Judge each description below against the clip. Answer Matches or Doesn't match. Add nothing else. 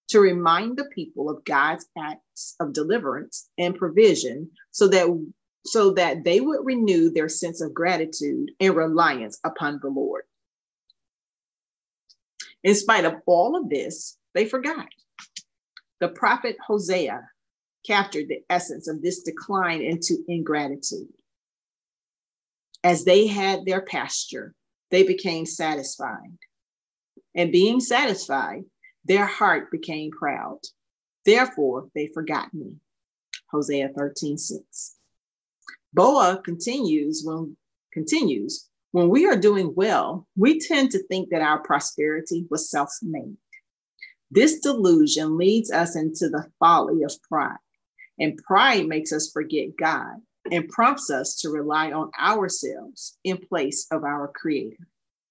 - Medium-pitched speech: Matches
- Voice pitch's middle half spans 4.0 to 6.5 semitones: Matches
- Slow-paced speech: Matches